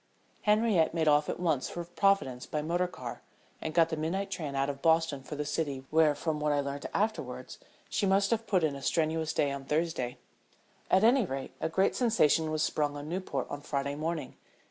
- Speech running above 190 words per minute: Yes, fast, 205 wpm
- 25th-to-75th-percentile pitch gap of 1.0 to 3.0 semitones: No, average, 3.8 semitones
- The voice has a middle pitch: Yes, medium, 160 Hz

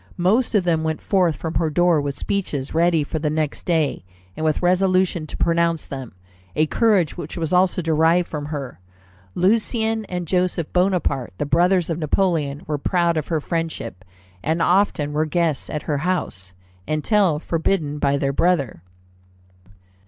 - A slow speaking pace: No, average, 160 wpm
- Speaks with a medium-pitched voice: Yes, medium, 165 Hz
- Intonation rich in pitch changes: No, average, 3.2 semitones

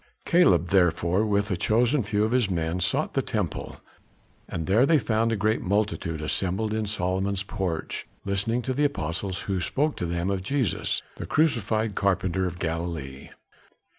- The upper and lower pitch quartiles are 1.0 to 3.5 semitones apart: No, average, 4.0 semitones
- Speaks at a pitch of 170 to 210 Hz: No, low, 100 Hz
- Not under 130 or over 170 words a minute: Yes, average, 165 wpm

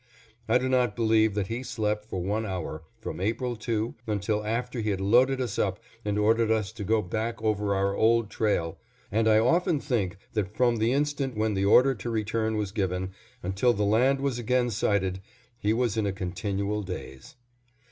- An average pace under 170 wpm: No, average, 190 wpm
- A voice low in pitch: Yes, low, 110 Hz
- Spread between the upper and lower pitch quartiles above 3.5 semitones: No, average, 2.9 semitones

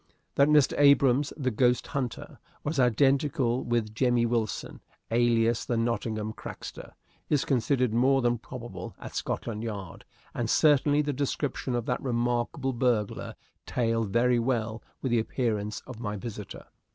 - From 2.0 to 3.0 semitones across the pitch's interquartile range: Yes, average, 2.7 semitones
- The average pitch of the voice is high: No, low, 120 Hz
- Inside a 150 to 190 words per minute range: No, average, 140 wpm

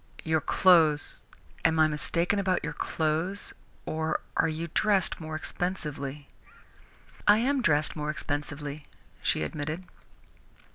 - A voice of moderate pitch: Yes, medium, 160 Hz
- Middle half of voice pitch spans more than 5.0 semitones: No, average, 3.1 semitones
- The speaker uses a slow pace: Yes, slow, 115 wpm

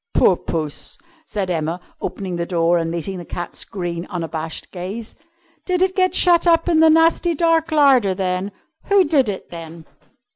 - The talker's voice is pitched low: No, high, 190 Hz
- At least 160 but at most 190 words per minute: Yes, average, 170 wpm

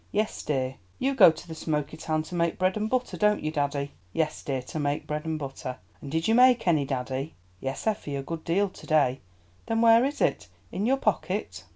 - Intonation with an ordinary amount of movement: No, wide, 6.8 semitones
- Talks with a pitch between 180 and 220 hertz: No, medium, 160 Hz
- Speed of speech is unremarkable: No, fast, 220 wpm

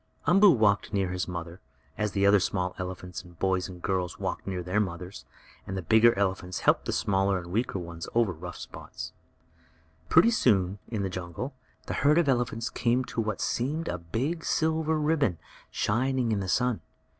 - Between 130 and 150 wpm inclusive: No, average, 180 wpm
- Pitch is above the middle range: No, low, 100 Hz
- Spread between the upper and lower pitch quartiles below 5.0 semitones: No, average, 5.3 semitones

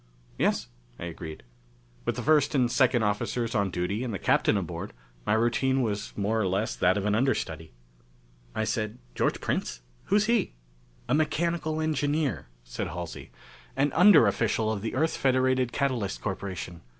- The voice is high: No, low, 115 Hz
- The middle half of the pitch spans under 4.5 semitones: No, wide, 5.6 semitones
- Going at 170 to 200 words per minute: No, average, 160 wpm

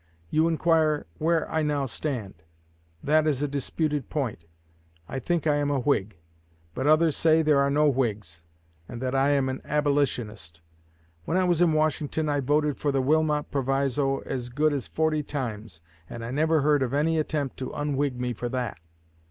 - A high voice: No, medium, 145 Hz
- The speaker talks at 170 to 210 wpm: Yes, average, 180 wpm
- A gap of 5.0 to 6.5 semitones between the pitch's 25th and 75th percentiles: No, average, 3.1 semitones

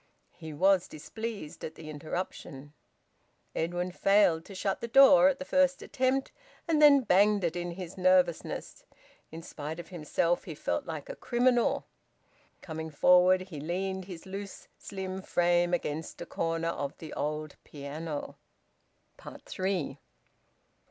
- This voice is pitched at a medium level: Yes, medium, 175 Hz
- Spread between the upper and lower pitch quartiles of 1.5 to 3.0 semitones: No, average, 3.8 semitones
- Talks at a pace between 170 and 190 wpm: No, average, 140 wpm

